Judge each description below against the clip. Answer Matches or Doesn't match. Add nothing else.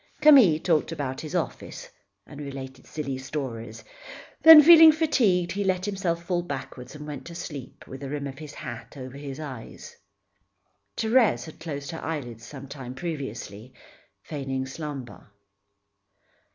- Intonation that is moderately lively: Matches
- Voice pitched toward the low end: Doesn't match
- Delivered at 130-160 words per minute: Matches